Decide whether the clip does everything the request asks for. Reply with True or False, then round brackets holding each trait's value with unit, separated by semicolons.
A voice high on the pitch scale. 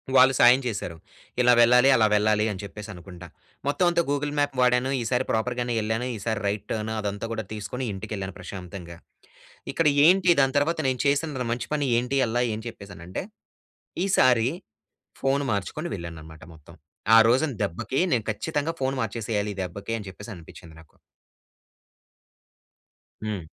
False (115 Hz)